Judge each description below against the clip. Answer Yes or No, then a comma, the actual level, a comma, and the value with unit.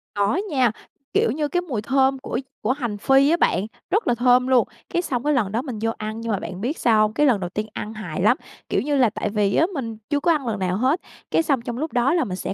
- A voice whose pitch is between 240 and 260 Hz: Yes, high, 245 Hz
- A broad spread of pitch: No, average, 4.6 semitones